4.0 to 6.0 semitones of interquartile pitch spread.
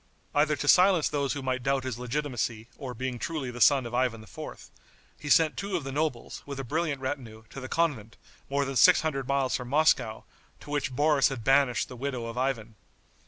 No: average, 3.0 semitones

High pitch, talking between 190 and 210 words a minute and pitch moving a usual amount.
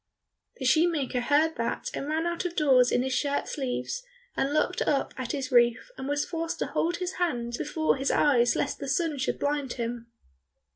Yes: very high, 285 Hz; average, 195 wpm; average, 4.1 semitones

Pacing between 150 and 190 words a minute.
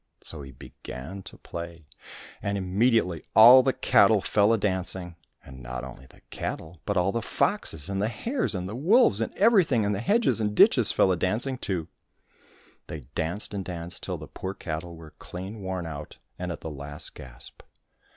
Yes: average, 185 wpm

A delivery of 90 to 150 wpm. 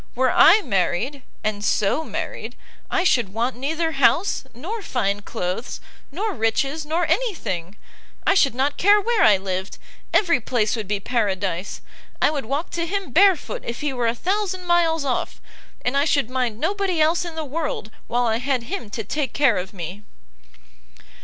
No: average, 175 wpm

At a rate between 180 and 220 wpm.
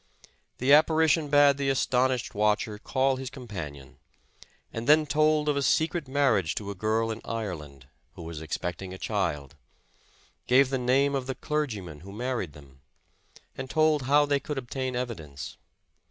No: average, 160 wpm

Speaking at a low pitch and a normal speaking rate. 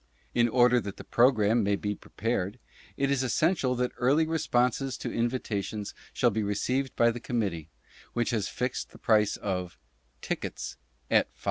Yes: low, 120 Hz; average, 165 wpm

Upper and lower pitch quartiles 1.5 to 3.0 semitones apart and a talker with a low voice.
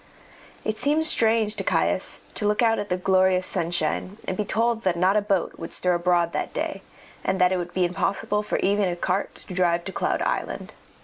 No: average, 2.7 semitones; high, 190 Hz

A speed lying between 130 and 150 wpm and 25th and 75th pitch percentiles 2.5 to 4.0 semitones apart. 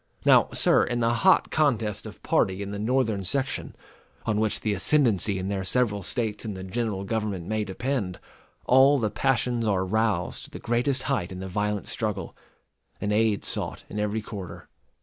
No: average, 180 wpm; average, 3.5 semitones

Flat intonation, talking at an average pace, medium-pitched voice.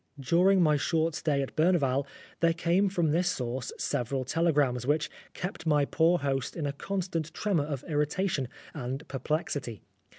No: average, 3.7 semitones; average, 160 wpm; medium, 150 Hz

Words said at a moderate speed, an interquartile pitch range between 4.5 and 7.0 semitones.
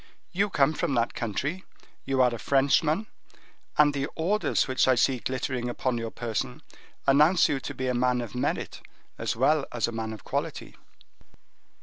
No: average, 170 wpm; average, 3.6 semitones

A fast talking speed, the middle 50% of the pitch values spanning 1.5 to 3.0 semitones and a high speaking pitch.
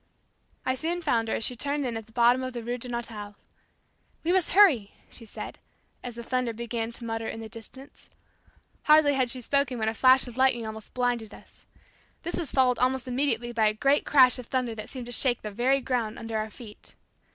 Yes: fast, 215 wpm; average, 2.7 semitones; high, 245 Hz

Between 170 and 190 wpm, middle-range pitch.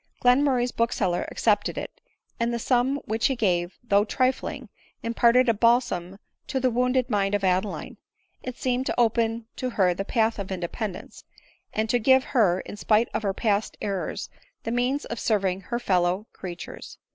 No: average, 175 wpm; high, 225 Hz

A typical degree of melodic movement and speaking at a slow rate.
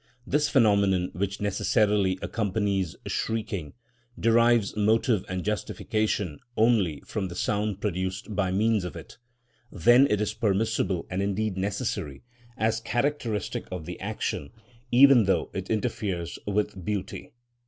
Yes: average, 3.0 semitones; slow, 125 wpm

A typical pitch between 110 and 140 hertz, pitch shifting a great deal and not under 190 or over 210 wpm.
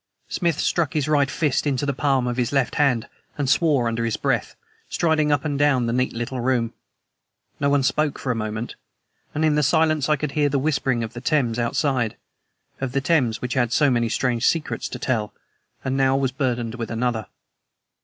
No: low, 135 Hz; average, 3.6 semitones; fast, 205 wpm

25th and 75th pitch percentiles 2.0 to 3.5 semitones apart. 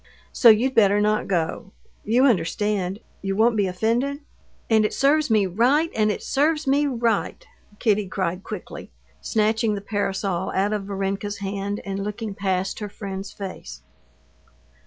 Yes: average, 2.8 semitones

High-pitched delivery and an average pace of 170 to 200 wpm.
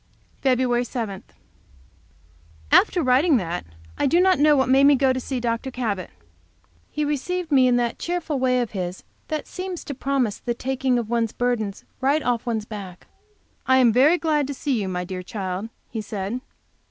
Yes: very high, 250 Hz; average, 175 wpm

